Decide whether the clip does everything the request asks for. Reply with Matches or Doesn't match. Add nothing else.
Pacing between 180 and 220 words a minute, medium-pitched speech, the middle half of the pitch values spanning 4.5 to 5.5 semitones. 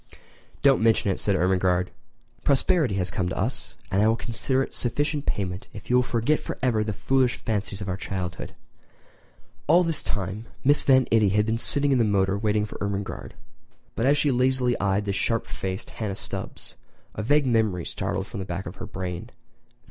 Doesn't match